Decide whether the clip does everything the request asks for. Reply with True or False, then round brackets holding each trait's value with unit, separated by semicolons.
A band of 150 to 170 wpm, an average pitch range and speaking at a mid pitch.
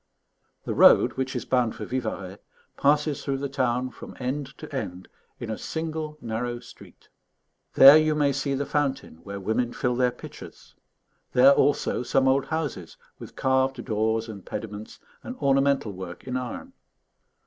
False (160 wpm; 3.8 semitones; 130 Hz)